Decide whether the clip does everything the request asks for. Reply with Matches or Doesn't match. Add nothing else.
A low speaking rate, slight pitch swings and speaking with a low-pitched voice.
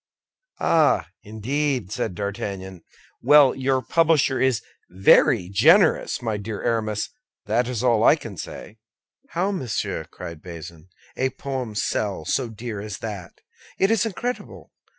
Doesn't match